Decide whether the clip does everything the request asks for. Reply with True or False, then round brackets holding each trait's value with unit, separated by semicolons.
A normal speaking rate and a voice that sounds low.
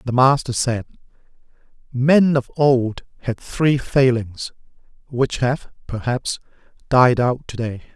False (120 wpm; 125 Hz)